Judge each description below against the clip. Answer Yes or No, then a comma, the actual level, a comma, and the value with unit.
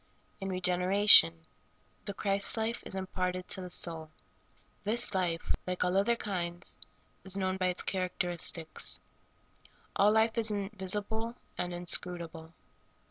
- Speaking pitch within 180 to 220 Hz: Yes, medium, 185 Hz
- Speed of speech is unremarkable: No, slow, 130 wpm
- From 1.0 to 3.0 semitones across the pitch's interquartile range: Yes, narrow, 2.5 semitones